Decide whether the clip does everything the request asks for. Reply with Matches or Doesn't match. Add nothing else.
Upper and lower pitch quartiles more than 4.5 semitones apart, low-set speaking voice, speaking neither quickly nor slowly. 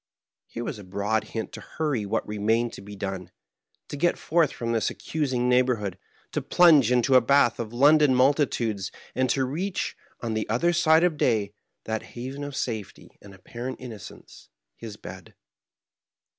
Matches